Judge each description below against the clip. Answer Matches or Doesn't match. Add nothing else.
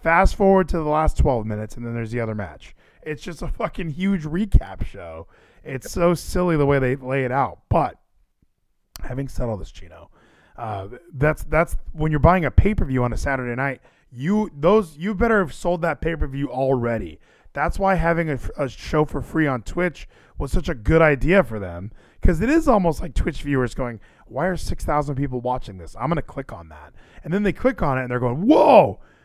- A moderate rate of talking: Doesn't match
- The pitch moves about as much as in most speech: Doesn't match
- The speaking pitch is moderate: Matches